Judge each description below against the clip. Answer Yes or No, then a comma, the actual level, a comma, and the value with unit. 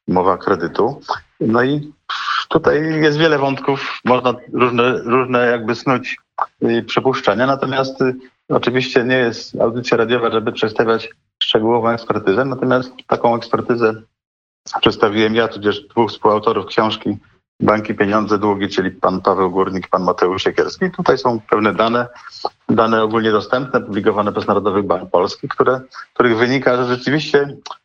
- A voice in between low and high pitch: No, low, 120 Hz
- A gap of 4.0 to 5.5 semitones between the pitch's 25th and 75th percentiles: No, average, 2.8 semitones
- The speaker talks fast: No, average, 130 wpm